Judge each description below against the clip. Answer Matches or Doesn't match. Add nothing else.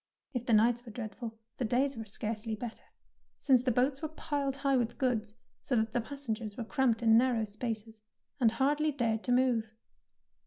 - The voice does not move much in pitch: Doesn't match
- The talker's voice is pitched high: Matches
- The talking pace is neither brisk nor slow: Matches